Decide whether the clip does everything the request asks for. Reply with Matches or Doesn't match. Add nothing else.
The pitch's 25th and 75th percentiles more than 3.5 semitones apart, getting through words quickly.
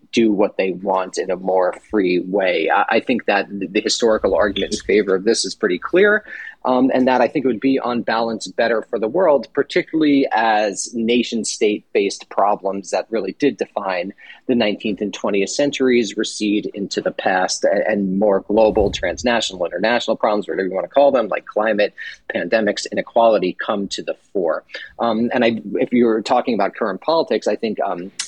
Doesn't match